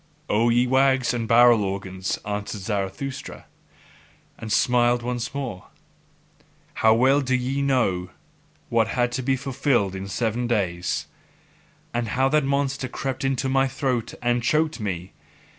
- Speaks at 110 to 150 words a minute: Yes, average, 140 wpm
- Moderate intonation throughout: Yes, average, 3.9 semitones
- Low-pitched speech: Yes, low, 120 Hz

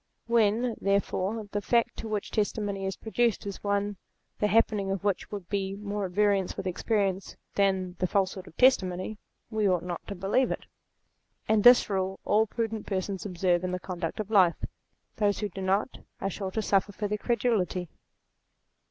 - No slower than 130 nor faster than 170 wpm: No, average, 180 wpm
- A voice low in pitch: No, high, 200 Hz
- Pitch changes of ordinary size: No, narrow, 2.2 semitones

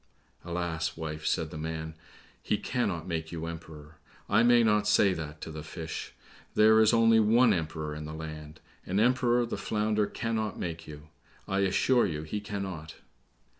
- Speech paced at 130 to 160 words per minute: No, average, 170 wpm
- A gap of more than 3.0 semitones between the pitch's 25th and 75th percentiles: Yes, wide, 5.5 semitones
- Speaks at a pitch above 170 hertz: No, very low, 85 Hz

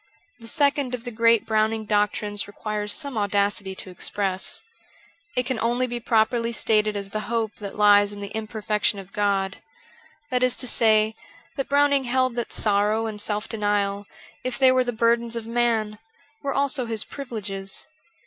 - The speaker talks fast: No, average, 170 wpm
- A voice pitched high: Yes, high, 220 Hz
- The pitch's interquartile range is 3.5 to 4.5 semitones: No, average, 2.8 semitones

